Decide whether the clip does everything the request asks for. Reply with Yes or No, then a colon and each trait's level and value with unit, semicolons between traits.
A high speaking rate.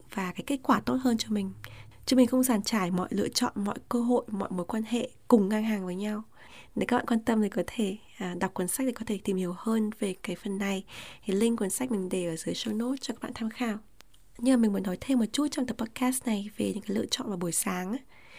Yes: fast, 275 wpm